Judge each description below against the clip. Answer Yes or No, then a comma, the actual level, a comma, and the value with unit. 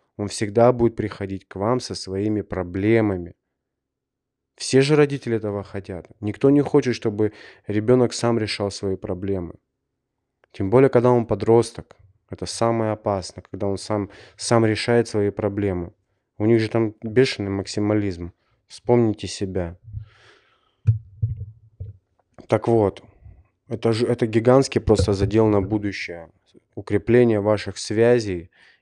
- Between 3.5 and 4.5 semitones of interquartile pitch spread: No, average, 2.8 semitones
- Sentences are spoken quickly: No, average, 125 wpm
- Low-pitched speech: Yes, low, 105 Hz